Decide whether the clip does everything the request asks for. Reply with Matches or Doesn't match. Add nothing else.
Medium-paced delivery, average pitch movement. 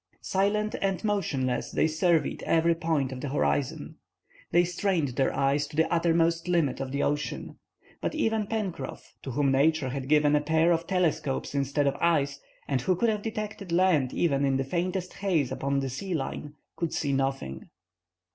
Matches